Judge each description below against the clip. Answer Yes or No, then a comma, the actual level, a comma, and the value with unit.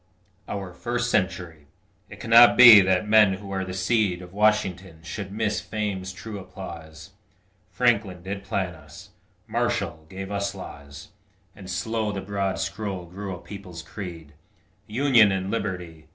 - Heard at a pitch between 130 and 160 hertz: No, very low, 95 Hz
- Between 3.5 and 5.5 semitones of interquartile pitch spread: No, average, 2.8 semitones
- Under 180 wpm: Yes, average, 145 wpm